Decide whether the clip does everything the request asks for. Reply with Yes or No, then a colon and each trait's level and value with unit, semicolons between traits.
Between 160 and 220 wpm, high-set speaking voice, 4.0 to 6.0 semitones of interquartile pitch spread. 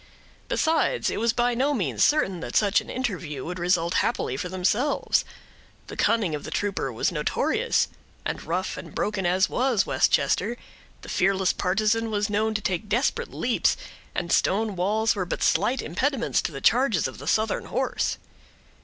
Yes: average, 170 wpm; high, 205 Hz; average, 4.3 semitones